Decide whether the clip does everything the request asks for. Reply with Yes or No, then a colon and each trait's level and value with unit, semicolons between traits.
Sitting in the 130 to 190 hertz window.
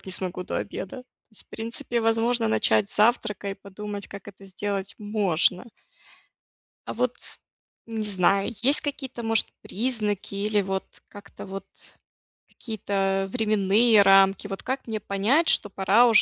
No: high, 205 Hz